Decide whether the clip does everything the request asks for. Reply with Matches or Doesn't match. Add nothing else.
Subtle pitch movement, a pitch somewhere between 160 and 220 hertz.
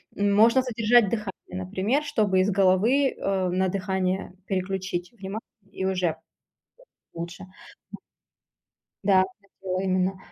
Matches